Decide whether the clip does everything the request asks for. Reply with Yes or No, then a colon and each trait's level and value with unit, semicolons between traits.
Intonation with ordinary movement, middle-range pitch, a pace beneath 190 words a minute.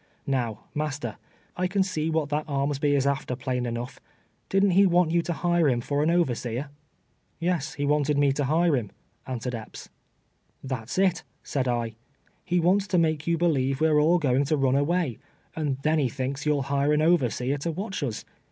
No: average, 4.0 semitones; medium, 145 Hz; average, 195 wpm